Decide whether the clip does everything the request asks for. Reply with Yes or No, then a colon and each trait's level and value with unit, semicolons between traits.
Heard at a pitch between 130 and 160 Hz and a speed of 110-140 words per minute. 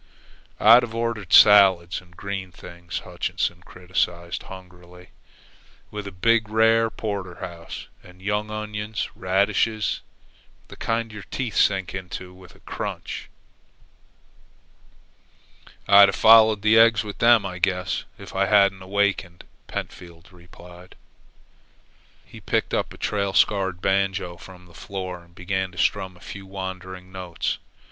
No: very low, 95 Hz; slow, 135 wpm